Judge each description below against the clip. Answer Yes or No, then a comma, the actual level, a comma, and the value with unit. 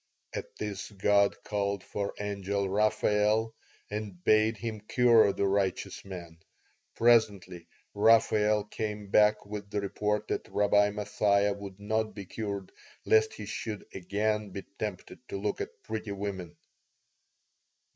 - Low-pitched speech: Yes, low, 105 Hz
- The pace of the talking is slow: Yes, slow, 130 wpm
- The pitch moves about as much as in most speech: No, narrow, 1.3 semitones